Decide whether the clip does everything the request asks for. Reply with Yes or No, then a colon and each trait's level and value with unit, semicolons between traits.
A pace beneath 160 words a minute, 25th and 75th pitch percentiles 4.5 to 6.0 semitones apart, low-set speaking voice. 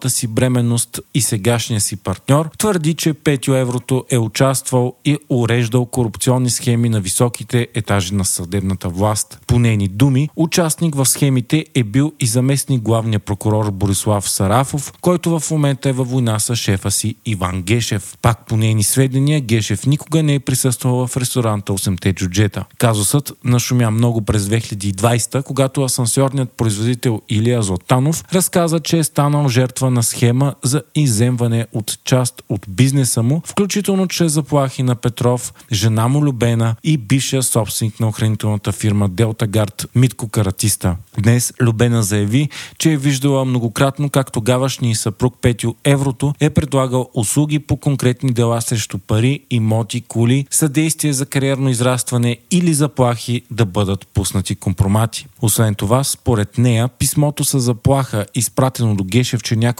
No: average, 145 wpm; average, 3.5 semitones; low, 125 Hz